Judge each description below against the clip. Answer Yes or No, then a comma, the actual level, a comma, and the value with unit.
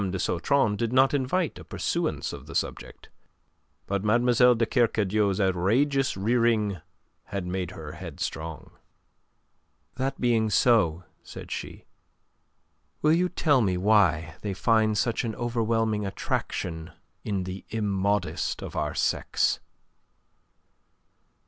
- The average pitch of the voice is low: Yes, low, 105 Hz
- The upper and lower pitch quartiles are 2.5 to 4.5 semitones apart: Yes, average, 4.0 semitones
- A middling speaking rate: No, slow, 115 wpm